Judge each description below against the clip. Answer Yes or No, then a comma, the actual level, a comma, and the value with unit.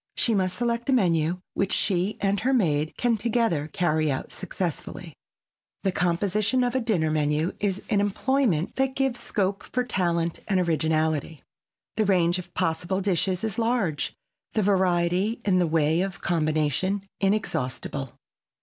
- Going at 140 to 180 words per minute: Yes, average, 150 wpm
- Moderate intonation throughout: Yes, average, 4.6 semitones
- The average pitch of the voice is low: No, medium, 185 Hz